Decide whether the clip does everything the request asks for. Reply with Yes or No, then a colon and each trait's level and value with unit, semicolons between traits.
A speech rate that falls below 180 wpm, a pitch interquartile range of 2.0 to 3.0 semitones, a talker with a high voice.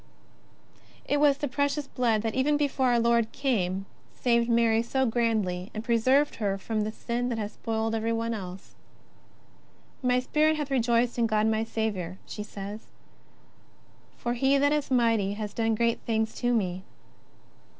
Yes: average, 165 wpm; average, 2.7 semitones; high, 230 Hz